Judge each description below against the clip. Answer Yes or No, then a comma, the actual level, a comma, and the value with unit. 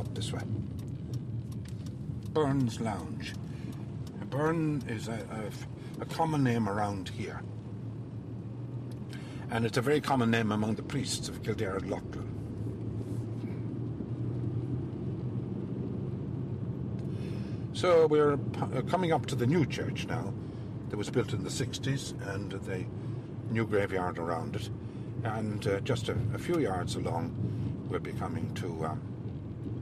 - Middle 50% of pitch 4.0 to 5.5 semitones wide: No, average, 3.0 semitones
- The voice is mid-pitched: No, low, 120 Hz